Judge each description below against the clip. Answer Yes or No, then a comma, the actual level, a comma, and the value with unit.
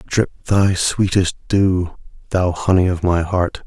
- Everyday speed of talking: Yes, average, 145 wpm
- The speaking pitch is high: No, very low, 90 Hz